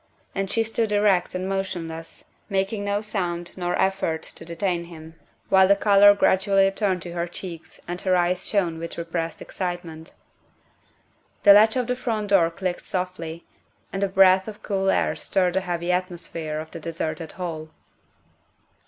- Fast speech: No, average, 165 wpm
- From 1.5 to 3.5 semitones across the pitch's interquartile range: Yes, average, 2.7 semitones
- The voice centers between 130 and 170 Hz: No, medium, 185 Hz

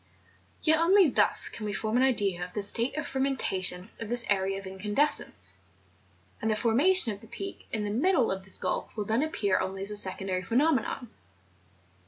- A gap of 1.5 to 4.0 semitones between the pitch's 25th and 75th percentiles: No, wide, 5.4 semitones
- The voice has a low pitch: No, high, 220 Hz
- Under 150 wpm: No, average, 190 wpm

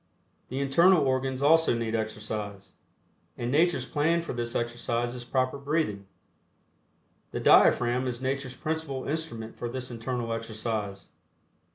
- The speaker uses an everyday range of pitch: Yes, average, 3.3 semitones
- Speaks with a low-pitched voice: Yes, low, 125 Hz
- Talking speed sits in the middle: No, slow, 130 wpm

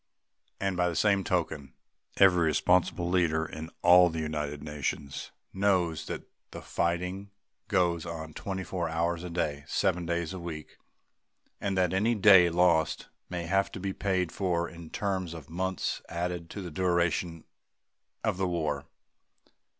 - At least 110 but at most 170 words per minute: Yes, average, 150 wpm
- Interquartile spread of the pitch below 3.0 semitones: Yes, narrow, 2.4 semitones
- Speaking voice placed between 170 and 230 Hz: No, very low, 85 Hz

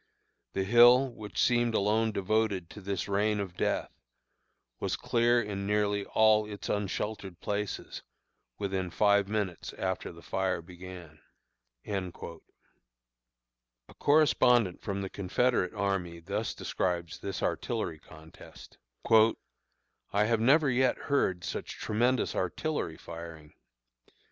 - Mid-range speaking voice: No, low, 100 Hz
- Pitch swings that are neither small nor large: Yes, average, 3.9 semitones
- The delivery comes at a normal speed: No, slow, 115 wpm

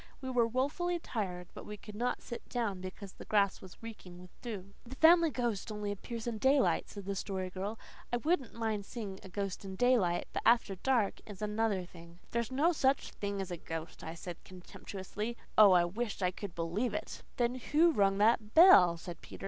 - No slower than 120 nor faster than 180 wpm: No, fast, 205 wpm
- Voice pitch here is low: No, high, 210 Hz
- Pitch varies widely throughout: No, average, 4.4 semitones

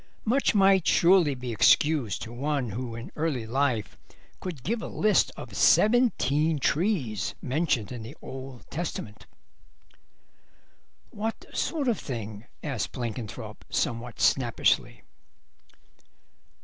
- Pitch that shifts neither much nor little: No, wide, 6.9 semitones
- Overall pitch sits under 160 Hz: Yes, low, 135 Hz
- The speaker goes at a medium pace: No, slow, 110 wpm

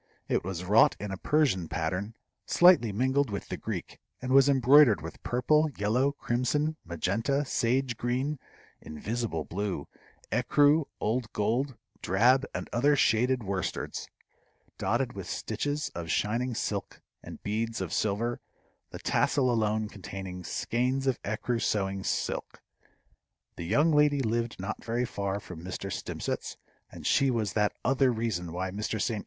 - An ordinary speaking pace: Yes, average, 145 wpm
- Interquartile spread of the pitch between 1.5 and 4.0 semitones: No, average, 5.0 semitones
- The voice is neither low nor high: No, low, 115 Hz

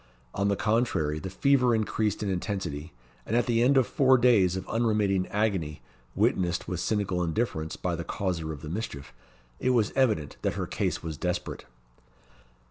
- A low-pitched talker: Yes, low, 100 Hz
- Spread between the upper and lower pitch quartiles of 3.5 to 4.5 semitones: No, average, 5.2 semitones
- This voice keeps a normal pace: Yes, average, 170 wpm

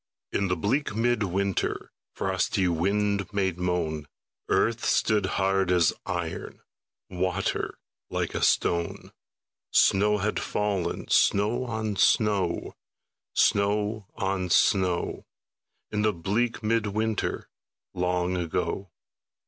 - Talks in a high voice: No, low, 100 Hz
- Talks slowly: Yes, slow, 105 wpm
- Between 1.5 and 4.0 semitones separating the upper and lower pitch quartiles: Yes, average, 2.7 semitones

